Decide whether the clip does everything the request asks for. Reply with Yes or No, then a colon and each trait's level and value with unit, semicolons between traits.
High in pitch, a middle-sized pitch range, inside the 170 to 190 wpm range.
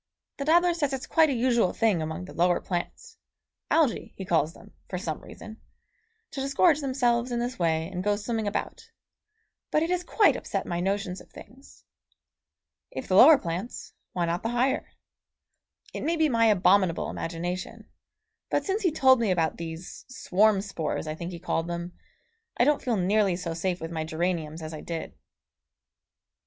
No: high, 200 Hz; wide, 7.1 semitones; average, 175 wpm